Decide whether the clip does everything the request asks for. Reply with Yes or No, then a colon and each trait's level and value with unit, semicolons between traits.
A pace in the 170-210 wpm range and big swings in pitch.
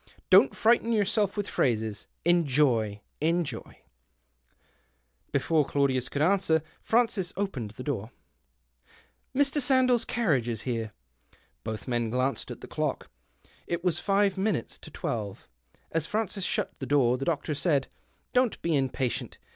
No: average, 145 wpm; wide, 8.7 semitones